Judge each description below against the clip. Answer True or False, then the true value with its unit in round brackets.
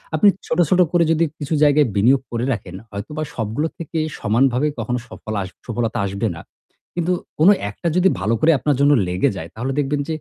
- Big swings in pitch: True (6.0 semitones)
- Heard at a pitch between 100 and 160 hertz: True (135 Hz)